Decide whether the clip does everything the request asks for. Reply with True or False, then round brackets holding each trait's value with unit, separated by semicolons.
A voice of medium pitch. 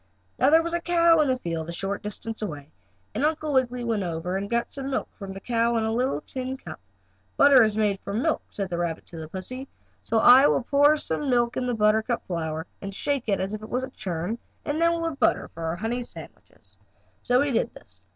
False (230 Hz)